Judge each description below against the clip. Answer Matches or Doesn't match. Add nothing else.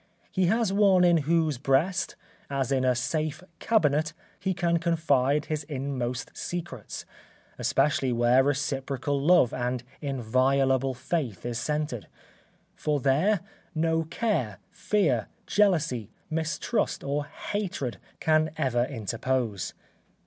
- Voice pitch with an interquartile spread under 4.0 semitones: Doesn't match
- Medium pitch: Matches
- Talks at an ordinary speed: Doesn't match